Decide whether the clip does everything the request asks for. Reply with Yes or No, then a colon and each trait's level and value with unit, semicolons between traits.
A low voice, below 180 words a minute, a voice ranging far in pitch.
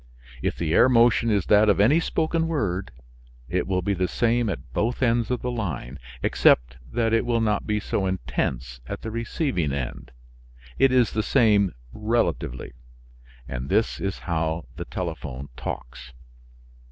Yes: low, 100 Hz; average, 160 wpm; wide, 6.7 semitones